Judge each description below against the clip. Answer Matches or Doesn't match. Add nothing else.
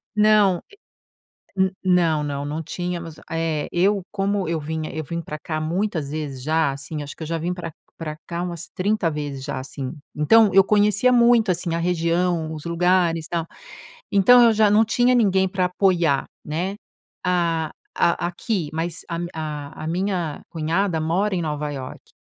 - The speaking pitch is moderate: Matches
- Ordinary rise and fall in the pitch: Matches